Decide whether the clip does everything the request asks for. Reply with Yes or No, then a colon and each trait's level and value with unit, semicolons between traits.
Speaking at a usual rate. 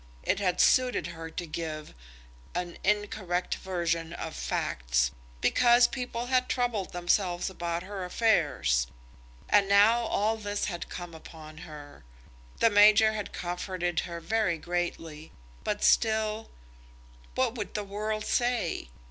No: slow, 130 wpm